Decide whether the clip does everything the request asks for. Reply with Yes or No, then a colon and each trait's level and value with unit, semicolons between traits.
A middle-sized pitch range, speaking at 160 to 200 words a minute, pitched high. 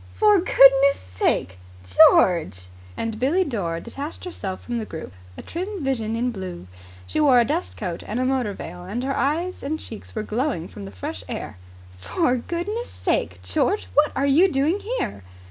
No: wide, 8.8 semitones; average, 180 wpm; very high, 255 Hz